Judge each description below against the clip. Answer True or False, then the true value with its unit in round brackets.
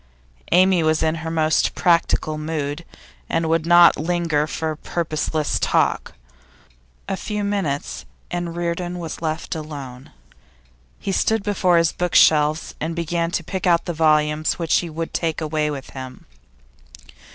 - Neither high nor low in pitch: True (165 Hz)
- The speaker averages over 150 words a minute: False (140 wpm)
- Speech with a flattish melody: True (2.0 semitones)